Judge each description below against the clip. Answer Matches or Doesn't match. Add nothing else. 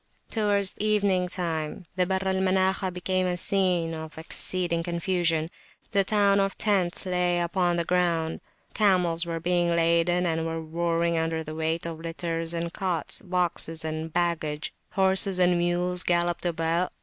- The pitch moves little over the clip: Matches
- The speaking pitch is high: Doesn't match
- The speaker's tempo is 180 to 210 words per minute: Doesn't match